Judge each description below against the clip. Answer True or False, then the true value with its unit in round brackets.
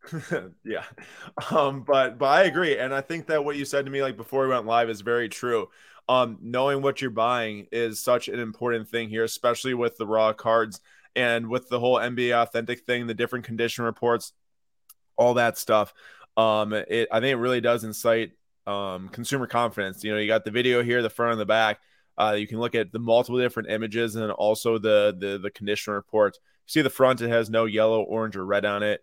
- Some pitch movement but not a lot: False (2.2 semitones)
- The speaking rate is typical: False (215 wpm)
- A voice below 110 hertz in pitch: False (115 Hz)